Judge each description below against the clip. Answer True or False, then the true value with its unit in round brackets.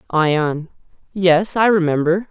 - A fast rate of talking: False (105 wpm)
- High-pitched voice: False (175 Hz)